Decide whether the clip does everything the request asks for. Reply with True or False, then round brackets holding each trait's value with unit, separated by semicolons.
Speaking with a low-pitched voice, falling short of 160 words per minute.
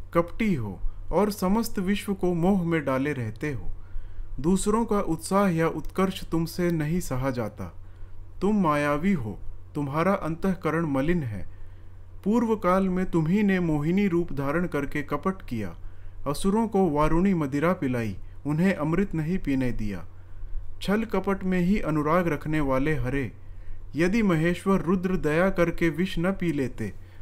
False (155 Hz; 145 wpm)